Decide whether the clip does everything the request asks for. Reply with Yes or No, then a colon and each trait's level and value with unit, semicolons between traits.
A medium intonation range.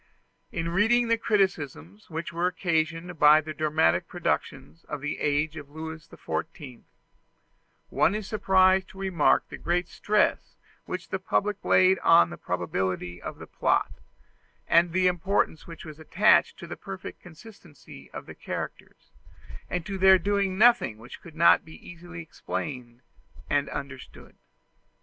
Yes: average, 4.2 semitones